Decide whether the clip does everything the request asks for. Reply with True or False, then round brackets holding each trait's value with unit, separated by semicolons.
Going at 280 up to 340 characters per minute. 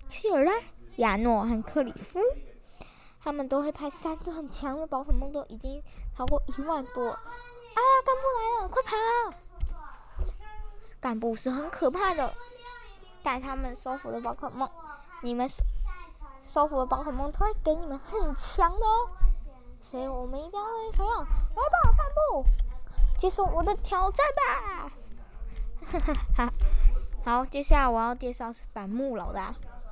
False (215 characters per minute)